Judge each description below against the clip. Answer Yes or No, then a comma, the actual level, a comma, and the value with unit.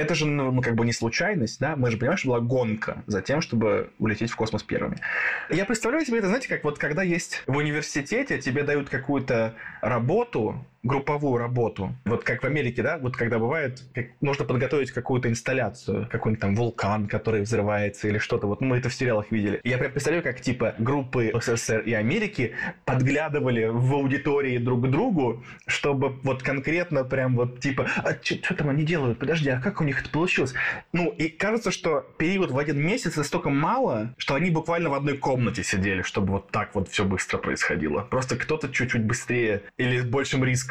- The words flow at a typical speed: No, fast, 190 wpm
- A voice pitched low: Yes, low, 130 Hz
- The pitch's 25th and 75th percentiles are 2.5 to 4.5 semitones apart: Yes, average, 4.0 semitones